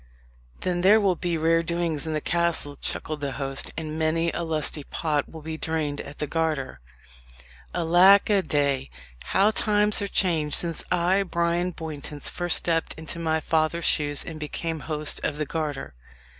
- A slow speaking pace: No, average, 170 wpm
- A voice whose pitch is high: No, medium, 160 Hz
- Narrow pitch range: Yes, narrow, 2.3 semitones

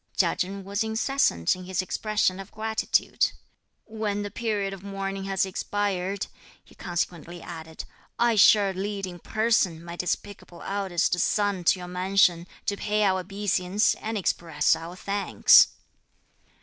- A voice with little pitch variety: Yes, narrow, 2.3 semitones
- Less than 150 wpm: Yes, average, 140 wpm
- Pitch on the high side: Yes, high, 195 Hz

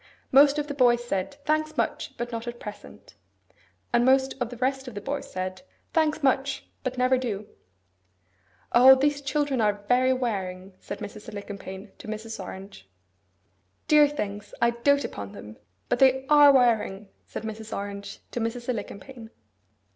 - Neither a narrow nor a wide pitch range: Yes, average, 4.6 semitones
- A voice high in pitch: Yes, high, 240 Hz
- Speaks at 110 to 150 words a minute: No, average, 160 wpm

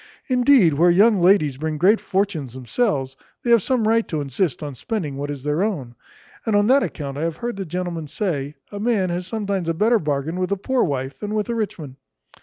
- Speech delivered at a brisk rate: Yes, fast, 220 wpm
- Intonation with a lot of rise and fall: Yes, wide, 6.5 semitones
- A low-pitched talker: No, medium, 180 Hz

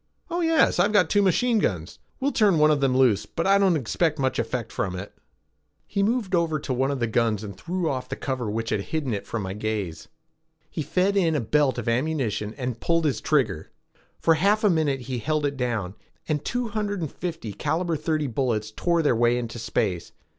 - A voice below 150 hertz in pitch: Yes, medium, 140 Hz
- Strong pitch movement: Yes, wide, 6.9 semitones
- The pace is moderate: No, fast, 215 wpm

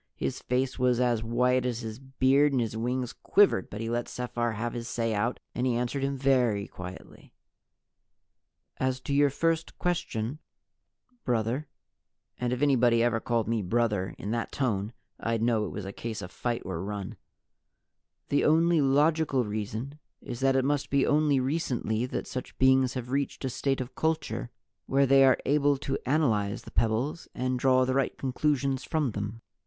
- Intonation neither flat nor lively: Yes, average, 3.1 semitones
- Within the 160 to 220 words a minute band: Yes, average, 175 wpm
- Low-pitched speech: Yes, low, 125 Hz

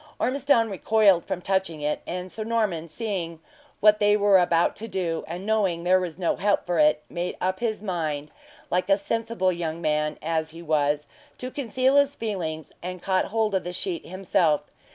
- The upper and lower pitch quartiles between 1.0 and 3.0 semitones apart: No, average, 4.4 semitones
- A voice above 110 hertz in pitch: Yes, medium, 185 Hz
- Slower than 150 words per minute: No, average, 185 wpm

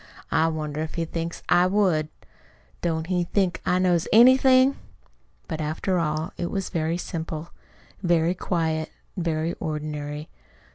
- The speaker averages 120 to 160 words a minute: Yes, average, 140 wpm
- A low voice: No, medium, 165 Hz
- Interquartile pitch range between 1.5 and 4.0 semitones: Yes, narrow, 2.4 semitones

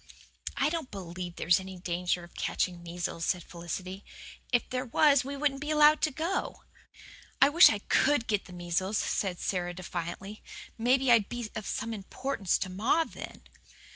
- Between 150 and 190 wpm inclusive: Yes, average, 170 wpm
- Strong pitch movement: Yes, wide, 7.2 semitones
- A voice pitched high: Yes, high, 205 Hz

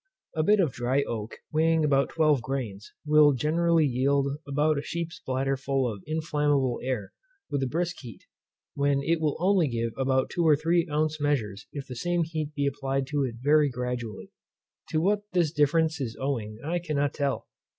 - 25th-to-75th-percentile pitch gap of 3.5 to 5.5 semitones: No, average, 3.1 semitones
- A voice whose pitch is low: No, medium, 145 Hz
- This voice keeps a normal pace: Yes, average, 180 wpm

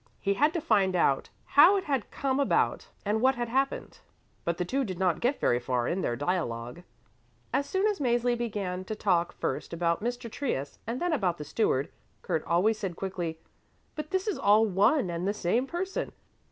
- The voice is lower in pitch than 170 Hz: No, high, 210 Hz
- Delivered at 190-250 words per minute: Yes, average, 195 wpm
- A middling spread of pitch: No, wide, 7.5 semitones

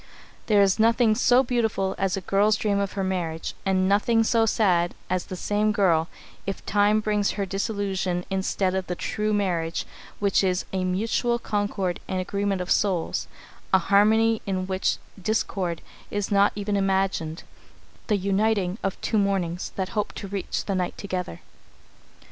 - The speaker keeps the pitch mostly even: Yes, narrow, 2.1 semitones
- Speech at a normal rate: Yes, average, 160 wpm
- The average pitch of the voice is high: Yes, high, 195 Hz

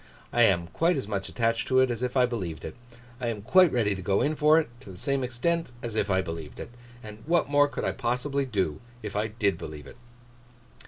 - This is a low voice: Yes, low, 115 Hz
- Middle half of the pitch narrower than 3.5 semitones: No, wide, 5.5 semitones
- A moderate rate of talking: No, fast, 235 wpm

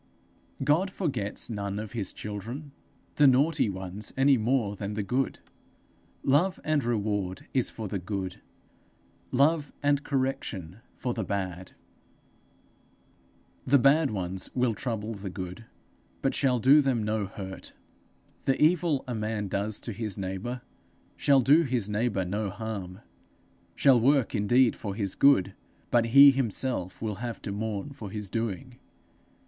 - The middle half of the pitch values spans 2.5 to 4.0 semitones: No, average, 5.0 semitones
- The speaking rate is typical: Yes, average, 145 wpm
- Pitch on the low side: Yes, low, 115 Hz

